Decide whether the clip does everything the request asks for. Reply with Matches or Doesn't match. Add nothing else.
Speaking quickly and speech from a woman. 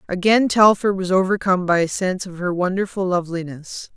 Doesn't match